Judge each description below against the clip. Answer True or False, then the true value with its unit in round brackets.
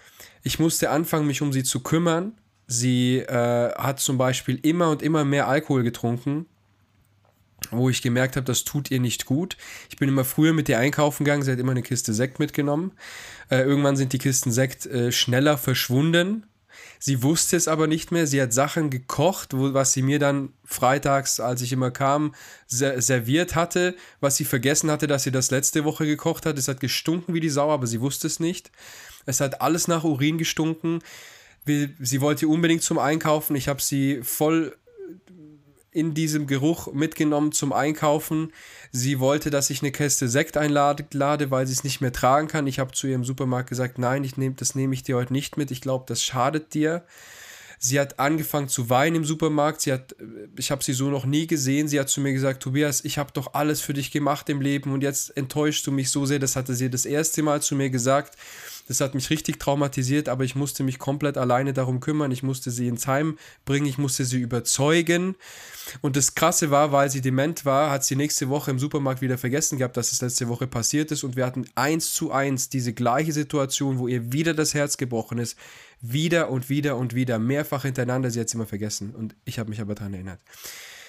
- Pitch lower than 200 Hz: True (140 Hz)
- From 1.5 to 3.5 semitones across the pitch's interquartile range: True (2.7 semitones)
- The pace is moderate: False (210 wpm)